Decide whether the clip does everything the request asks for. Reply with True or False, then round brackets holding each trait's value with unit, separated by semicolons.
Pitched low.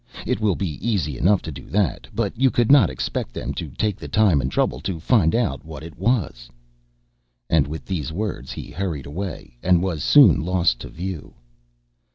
True (90 Hz)